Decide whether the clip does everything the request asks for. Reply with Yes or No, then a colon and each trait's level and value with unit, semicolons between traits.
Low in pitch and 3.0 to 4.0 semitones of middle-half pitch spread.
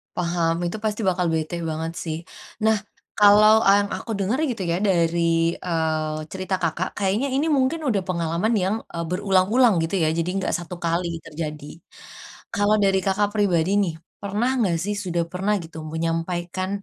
No: medium, 185 Hz; average, 3.5 semitones